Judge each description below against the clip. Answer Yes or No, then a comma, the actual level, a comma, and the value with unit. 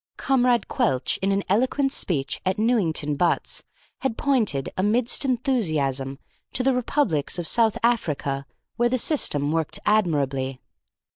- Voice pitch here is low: No, high, 195 Hz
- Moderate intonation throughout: No, wide, 9.0 semitones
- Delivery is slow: Yes, slow, 130 wpm